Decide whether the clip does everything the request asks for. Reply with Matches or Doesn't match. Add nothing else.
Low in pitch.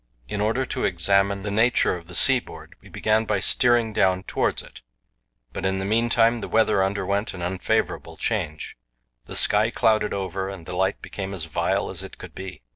Matches